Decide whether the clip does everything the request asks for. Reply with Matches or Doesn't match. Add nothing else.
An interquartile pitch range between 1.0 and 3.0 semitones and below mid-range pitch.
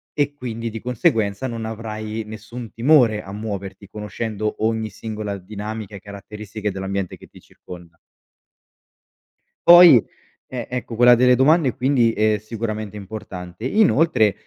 Matches